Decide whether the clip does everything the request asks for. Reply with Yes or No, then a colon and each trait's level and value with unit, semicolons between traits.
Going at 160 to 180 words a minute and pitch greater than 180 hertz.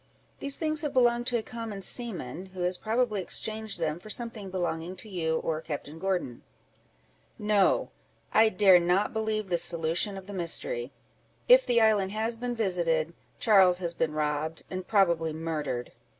Yes: average, 165 wpm; high, 190 Hz